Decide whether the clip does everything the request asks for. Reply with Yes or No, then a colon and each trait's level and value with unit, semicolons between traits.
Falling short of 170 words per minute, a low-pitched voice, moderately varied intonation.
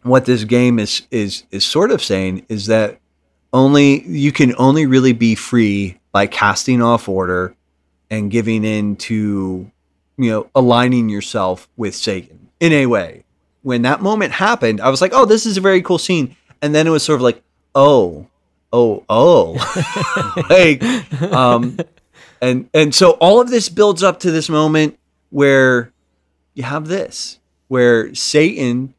No: average, 160 wpm; low, 125 Hz; wide, 6.1 semitones